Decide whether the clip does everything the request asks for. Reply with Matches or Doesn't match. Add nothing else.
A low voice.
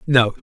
Matches